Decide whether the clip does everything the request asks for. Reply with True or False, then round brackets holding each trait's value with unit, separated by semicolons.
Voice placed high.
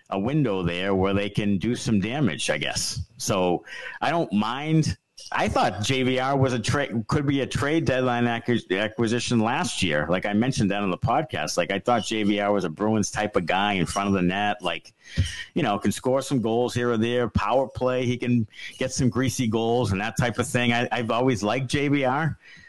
False (120 Hz)